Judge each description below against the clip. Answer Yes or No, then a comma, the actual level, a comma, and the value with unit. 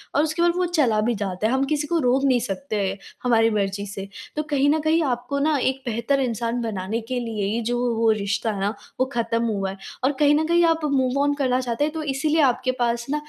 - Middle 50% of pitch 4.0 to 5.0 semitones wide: Yes, average, 4.7 semitones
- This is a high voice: Yes, high, 245 Hz